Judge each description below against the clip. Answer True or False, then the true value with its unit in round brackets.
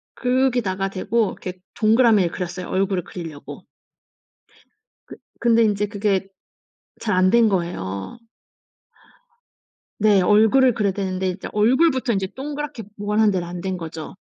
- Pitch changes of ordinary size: True (3.8 semitones)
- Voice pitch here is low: False (205 Hz)